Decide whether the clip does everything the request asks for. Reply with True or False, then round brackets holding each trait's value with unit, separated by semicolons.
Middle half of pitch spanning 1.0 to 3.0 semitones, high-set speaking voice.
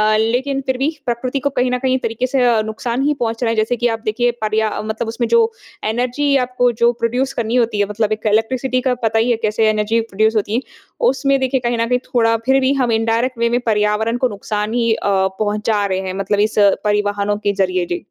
True (2.7 semitones; 230 Hz)